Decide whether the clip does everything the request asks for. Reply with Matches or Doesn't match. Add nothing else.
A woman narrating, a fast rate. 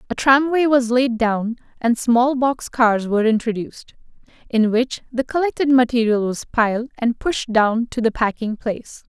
Doesn't match